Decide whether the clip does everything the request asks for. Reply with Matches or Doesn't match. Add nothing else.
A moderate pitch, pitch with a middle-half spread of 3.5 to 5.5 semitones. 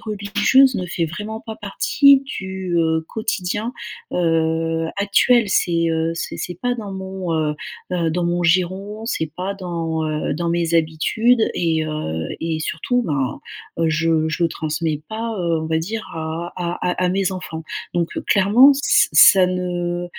Matches